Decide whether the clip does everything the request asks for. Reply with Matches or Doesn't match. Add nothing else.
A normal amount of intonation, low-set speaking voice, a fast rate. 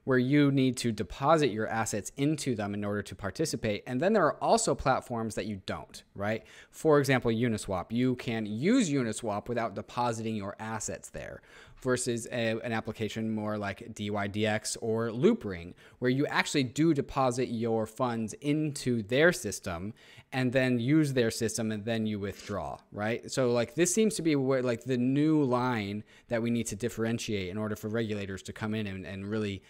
Doesn't match